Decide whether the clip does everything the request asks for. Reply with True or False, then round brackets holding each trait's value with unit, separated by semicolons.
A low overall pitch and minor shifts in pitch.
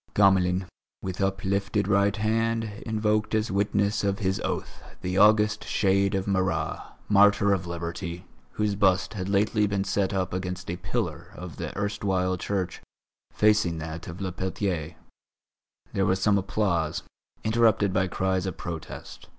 True (95 Hz; 2.0 semitones)